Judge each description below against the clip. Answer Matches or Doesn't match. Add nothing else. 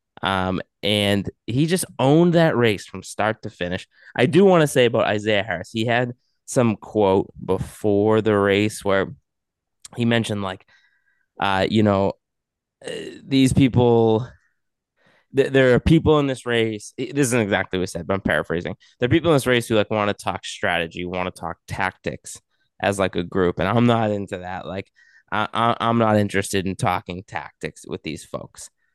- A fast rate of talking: Doesn't match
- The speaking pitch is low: Matches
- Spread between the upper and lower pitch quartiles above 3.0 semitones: Matches